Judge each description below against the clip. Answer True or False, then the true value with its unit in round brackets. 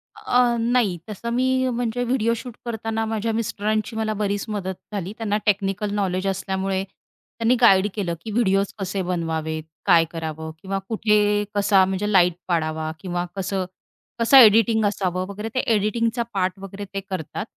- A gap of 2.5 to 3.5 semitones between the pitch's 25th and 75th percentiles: True (3.0 semitones)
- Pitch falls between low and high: False (205 Hz)